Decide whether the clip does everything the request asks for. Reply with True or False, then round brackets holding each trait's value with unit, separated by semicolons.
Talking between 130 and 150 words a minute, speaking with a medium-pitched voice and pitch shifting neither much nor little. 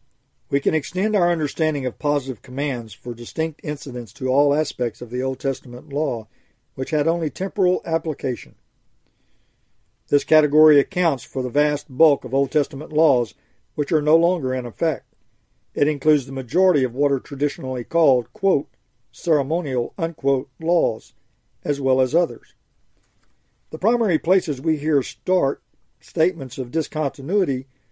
True (145 wpm; 145 Hz; 3.7 semitones)